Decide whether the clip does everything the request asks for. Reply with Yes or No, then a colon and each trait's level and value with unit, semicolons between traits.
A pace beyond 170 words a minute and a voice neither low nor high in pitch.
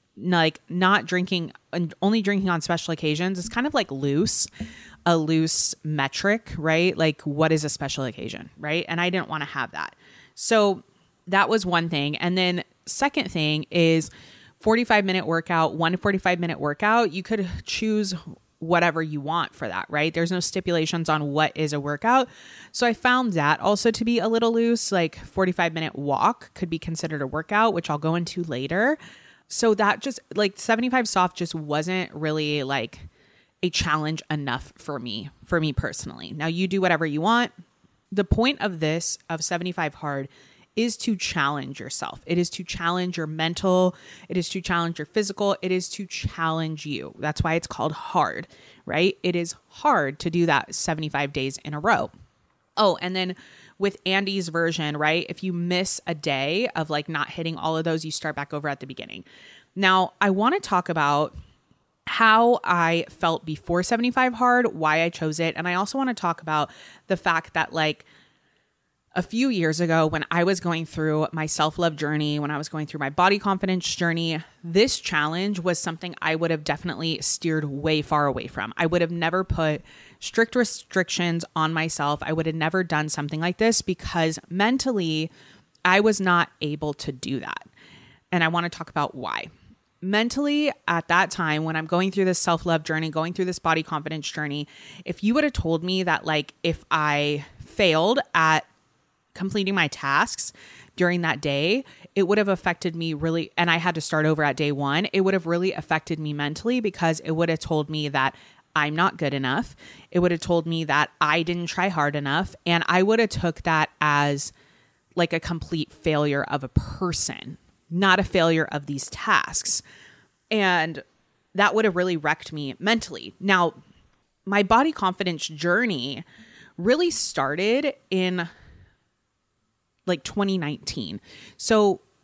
Yes: average, 180 wpm; medium, 170 Hz